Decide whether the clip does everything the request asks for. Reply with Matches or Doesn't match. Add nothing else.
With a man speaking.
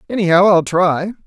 Matches